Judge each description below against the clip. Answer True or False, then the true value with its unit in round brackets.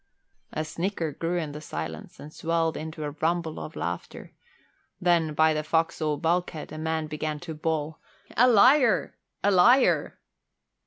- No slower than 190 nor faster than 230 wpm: False (150 wpm)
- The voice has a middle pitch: True (160 Hz)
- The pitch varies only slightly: True (2.2 semitones)